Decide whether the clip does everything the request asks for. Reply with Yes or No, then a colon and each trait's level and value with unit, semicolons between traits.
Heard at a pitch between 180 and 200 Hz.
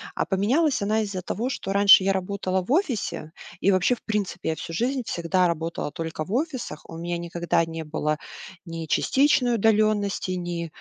Yes: high, 190 Hz